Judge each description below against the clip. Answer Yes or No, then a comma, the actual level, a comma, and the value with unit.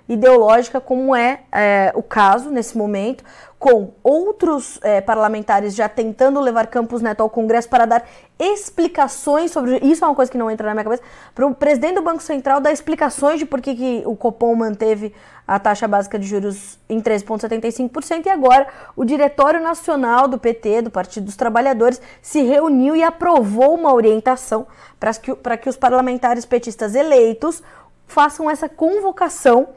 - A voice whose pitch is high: Yes, very high, 255 Hz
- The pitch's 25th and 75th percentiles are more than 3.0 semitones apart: Yes, average, 4.4 semitones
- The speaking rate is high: No, average, 165 wpm